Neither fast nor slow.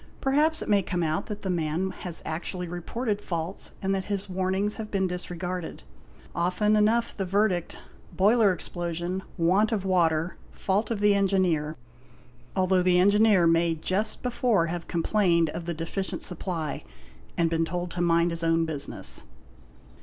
Yes: average, 160 wpm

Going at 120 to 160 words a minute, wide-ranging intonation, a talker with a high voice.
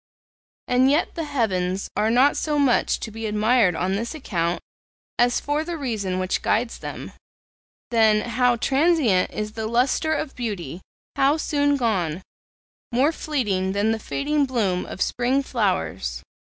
Yes: average, 150 wpm; wide, 5.8 semitones; high, 235 Hz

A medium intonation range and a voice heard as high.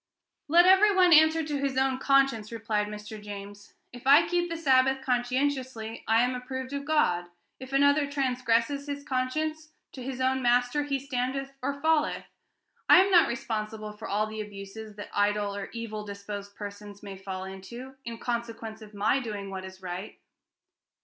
Yes: average, 5.0 semitones; high, 245 Hz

